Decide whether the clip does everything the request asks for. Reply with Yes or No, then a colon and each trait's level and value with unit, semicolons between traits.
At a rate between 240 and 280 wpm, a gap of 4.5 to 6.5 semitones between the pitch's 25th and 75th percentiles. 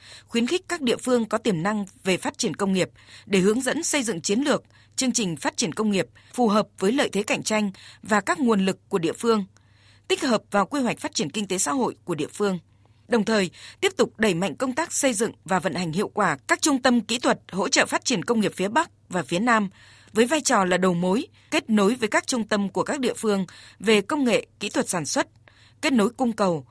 Yes: fast, 250 wpm; average, 5.0 semitones